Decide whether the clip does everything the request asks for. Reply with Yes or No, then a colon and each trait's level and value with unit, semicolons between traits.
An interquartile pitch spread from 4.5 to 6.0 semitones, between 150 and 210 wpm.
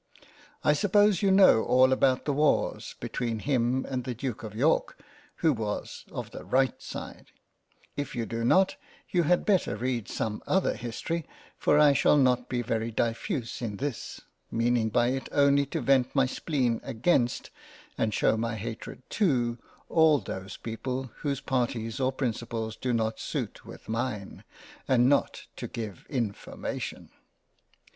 No: average, 3.6 semitones; average, 155 wpm